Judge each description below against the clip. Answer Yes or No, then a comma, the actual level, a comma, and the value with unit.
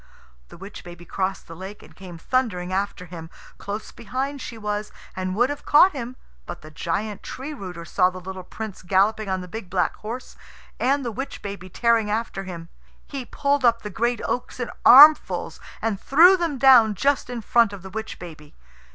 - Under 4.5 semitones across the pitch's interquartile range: No, average, 5.0 semitones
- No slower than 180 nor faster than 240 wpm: Yes, average, 195 wpm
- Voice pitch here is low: No, high, 210 Hz